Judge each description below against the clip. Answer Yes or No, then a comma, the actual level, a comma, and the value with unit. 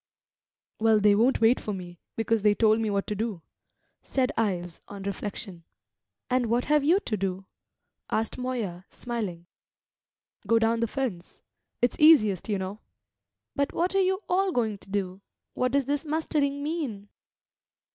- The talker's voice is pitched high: Yes, high, 225 Hz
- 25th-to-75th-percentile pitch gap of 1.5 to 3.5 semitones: No, average, 5.2 semitones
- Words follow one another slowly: No, average, 155 wpm